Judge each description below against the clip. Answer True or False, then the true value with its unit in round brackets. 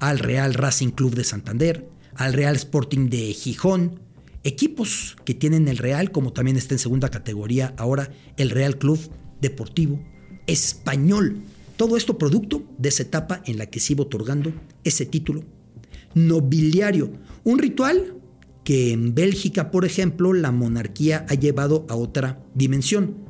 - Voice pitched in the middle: True (145 Hz)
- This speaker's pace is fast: False (145 wpm)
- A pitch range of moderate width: True (4.7 semitones)